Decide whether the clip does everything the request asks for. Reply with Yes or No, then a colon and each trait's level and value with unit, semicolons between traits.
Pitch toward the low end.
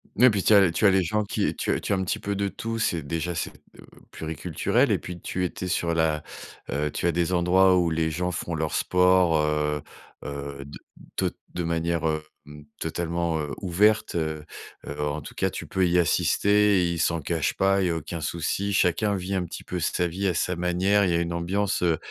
Yes: very low, 85 Hz